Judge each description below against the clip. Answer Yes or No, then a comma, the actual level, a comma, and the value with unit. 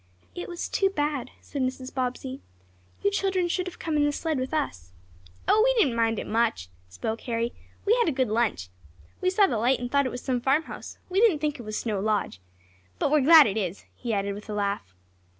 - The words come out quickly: Yes, fast, 220 wpm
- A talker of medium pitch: No, very high, 255 Hz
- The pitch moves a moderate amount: No, wide, 6.3 semitones